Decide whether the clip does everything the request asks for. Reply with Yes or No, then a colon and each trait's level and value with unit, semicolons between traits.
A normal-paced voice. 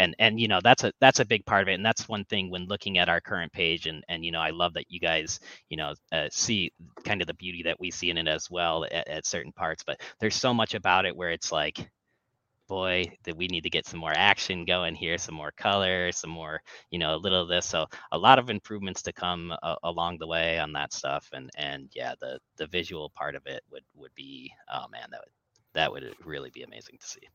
No: fast, 260 wpm